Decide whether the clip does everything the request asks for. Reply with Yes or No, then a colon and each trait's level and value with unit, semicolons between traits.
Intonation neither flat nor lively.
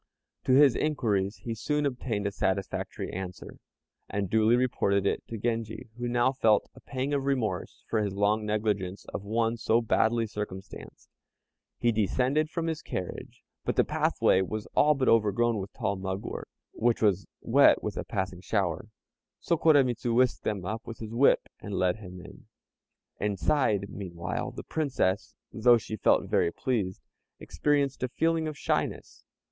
Yes: average, 4.3 semitones